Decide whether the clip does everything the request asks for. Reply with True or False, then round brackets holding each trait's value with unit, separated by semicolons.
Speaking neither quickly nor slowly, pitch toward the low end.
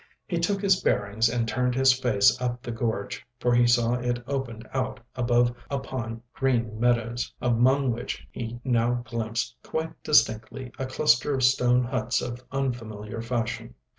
True (155 wpm; 120 Hz)